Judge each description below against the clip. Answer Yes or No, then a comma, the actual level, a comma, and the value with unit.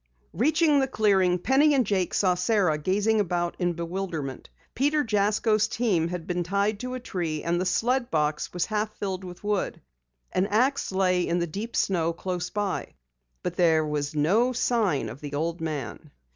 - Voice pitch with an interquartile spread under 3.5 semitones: No, average, 4.3 semitones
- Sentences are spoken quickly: No, average, 175 wpm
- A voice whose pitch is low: No, medium, 185 Hz